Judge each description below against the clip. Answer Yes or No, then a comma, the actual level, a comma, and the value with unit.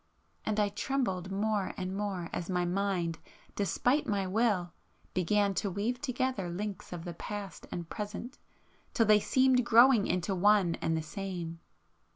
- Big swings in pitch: No, average, 3.2 semitones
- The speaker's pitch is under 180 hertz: No, high, 200 Hz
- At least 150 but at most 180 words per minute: Yes, average, 155 wpm